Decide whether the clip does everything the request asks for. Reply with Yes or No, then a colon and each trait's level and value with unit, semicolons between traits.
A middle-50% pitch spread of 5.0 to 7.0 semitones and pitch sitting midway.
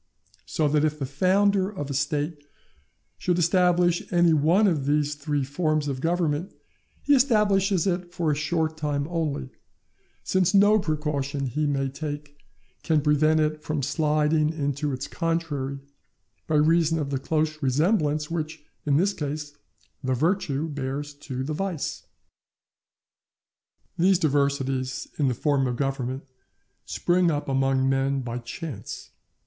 No: average, 3.1 semitones; medium, 150 Hz